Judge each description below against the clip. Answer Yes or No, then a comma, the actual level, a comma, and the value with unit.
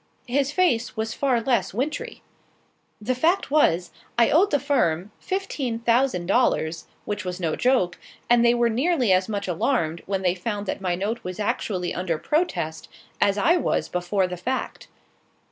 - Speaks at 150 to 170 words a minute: Yes, average, 165 wpm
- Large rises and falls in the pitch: Yes, wide, 6.2 semitones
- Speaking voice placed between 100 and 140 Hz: No, high, 220 Hz